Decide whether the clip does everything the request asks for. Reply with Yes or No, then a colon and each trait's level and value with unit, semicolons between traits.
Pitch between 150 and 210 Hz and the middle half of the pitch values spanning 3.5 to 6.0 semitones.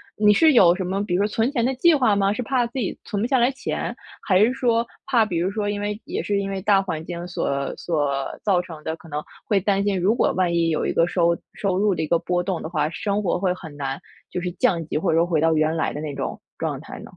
Yes: high, 190 Hz; average, 4.0 semitones